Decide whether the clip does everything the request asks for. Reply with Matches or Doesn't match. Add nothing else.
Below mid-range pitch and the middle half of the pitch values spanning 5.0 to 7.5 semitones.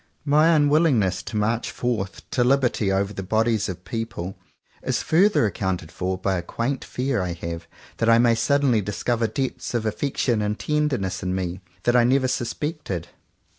Matches